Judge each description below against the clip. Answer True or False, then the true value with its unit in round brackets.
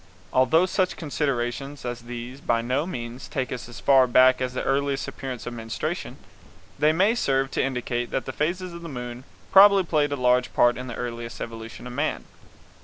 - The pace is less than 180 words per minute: False (195 wpm)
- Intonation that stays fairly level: False (3.2 semitones)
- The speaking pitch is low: True (130 Hz)